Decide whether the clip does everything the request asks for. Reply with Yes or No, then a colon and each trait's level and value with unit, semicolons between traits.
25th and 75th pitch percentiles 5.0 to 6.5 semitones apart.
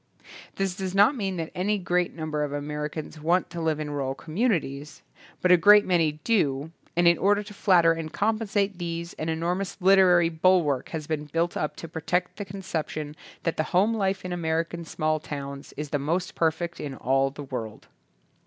No: average, 3.6 semitones